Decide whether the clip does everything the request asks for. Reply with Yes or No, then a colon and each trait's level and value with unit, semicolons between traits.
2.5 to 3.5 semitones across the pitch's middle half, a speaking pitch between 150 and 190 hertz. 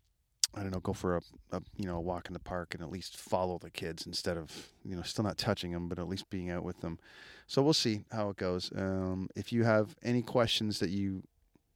No: average, 2.8 semitones; very low, 95 Hz